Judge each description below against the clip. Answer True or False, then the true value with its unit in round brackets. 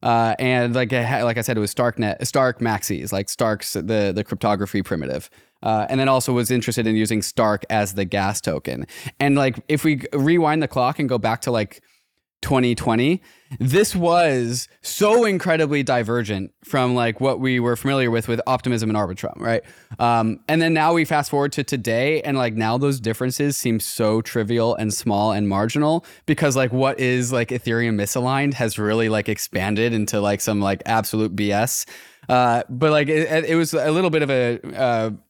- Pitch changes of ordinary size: True (3.9 semitones)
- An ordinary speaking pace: True (185 wpm)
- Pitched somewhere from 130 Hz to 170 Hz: False (120 Hz)